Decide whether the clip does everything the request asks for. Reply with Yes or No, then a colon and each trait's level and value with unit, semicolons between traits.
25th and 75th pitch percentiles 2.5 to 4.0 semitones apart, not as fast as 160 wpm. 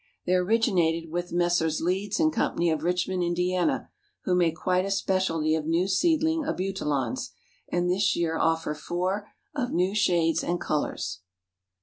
Yes: average, 2.8 semitones; average, 145 wpm